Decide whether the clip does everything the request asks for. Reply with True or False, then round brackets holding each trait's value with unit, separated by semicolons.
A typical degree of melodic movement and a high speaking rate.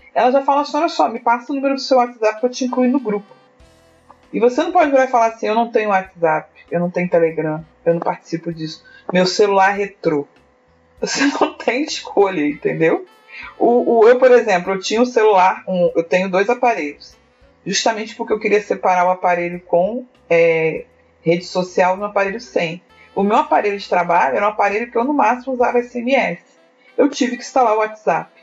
False (6.6 semitones; 200 wpm)